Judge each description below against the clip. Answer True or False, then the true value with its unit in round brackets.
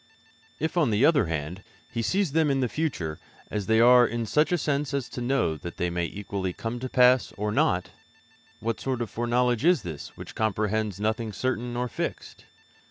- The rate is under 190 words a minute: False (195 wpm)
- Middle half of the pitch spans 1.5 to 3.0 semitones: False (4.4 semitones)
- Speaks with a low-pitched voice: True (120 Hz)